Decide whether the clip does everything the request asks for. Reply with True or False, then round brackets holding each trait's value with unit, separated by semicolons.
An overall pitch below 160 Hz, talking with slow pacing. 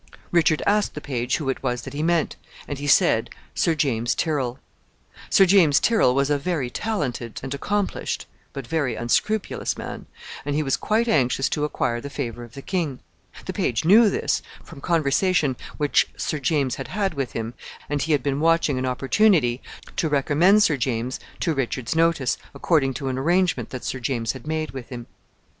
False (140 Hz; 185 wpm)